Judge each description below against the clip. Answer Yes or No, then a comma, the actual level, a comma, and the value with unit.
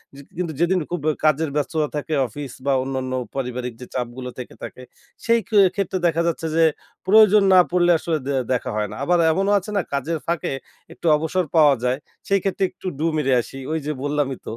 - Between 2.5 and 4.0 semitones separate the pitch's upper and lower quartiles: No, average, 4.7 semitones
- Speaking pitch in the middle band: Yes, medium, 155 Hz